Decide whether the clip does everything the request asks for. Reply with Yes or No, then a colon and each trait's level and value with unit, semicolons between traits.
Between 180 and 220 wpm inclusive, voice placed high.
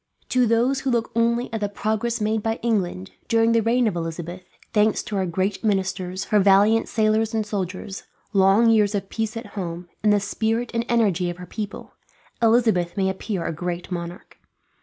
Yes: average, 185 wpm; high, 210 Hz